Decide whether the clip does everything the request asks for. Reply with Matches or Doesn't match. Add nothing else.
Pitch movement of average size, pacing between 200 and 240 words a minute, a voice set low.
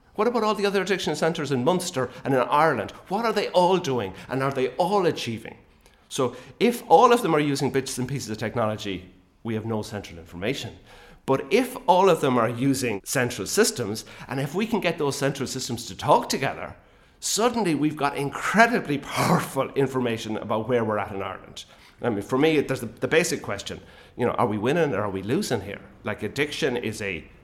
Doesn't match